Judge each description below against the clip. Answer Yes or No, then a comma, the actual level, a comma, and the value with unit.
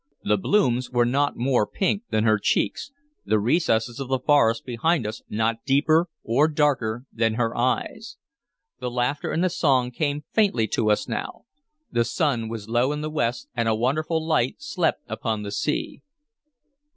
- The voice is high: No, low, 125 Hz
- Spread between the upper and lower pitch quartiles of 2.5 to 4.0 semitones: No, average, 4.7 semitones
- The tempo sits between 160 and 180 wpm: Yes, average, 170 wpm